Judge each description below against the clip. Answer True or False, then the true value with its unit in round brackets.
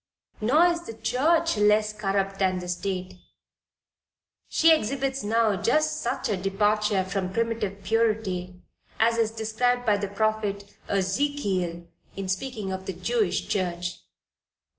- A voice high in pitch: True (210 Hz)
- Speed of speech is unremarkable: False (130 wpm)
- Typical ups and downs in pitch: True (3.3 semitones)